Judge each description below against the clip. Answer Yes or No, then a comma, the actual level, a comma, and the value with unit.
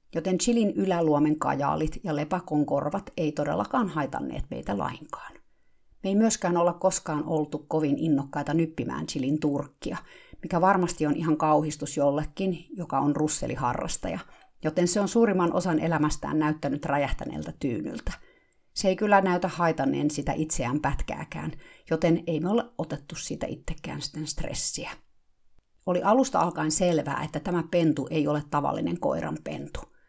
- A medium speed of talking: Yes, average, 140 wpm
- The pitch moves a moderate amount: Yes, average, 3.3 semitones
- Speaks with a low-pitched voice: No, medium, 155 Hz